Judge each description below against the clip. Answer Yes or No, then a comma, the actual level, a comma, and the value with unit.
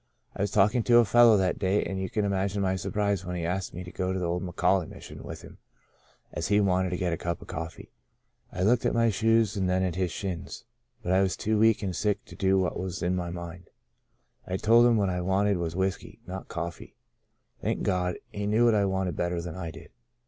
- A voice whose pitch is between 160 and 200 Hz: No, very low, 95 Hz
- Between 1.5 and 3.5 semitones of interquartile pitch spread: Yes, narrow, 2.4 semitones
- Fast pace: Yes, fast, 240 wpm